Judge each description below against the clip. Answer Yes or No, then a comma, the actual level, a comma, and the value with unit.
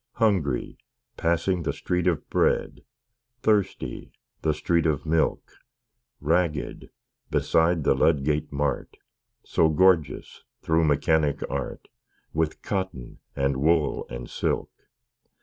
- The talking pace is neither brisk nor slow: No, slow, 105 wpm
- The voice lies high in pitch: No, very low, 80 Hz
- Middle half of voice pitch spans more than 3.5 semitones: No, average, 2.9 semitones